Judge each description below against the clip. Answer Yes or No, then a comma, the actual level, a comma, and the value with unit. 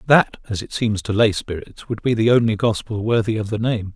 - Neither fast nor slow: No, fast, 245 wpm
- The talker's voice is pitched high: No, low, 110 Hz